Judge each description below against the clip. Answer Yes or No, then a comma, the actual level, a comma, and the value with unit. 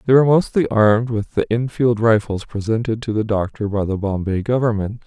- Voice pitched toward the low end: Yes, low, 110 Hz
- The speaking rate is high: No, average, 190 wpm